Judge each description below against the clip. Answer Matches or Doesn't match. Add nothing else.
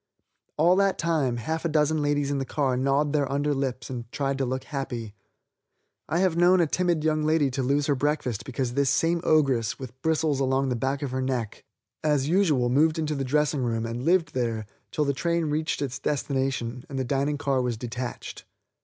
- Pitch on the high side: Doesn't match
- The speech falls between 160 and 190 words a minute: Doesn't match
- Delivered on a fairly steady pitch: Doesn't match